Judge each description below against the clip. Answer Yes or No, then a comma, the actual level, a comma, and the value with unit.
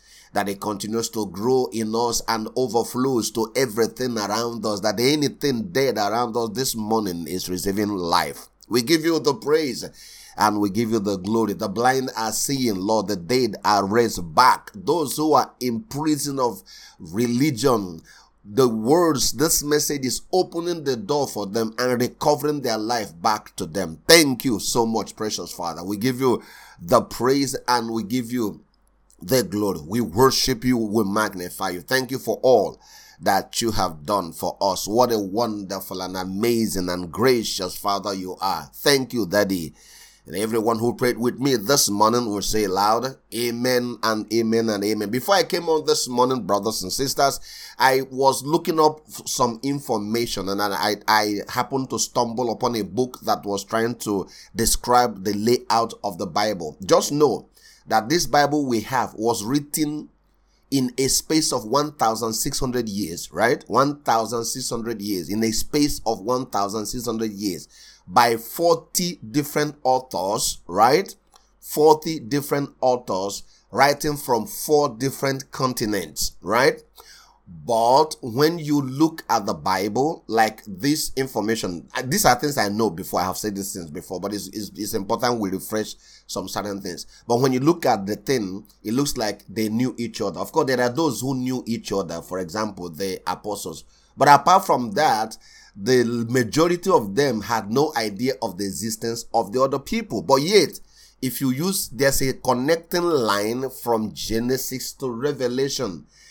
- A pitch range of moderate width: Yes, average, 4.2 semitones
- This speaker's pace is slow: No, average, 165 wpm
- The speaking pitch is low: Yes, low, 120 Hz